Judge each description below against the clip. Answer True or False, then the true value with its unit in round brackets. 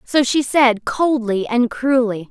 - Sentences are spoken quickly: False (155 wpm)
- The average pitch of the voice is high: True (245 Hz)